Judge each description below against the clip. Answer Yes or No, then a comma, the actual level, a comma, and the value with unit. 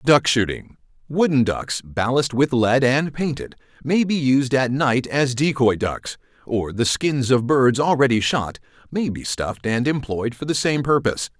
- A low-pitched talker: Yes, low, 130 Hz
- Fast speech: No, average, 170 wpm